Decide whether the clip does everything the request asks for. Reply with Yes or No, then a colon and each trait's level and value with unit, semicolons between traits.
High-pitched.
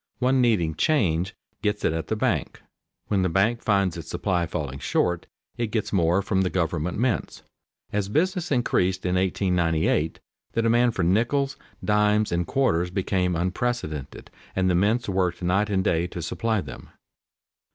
No: very low, 95 Hz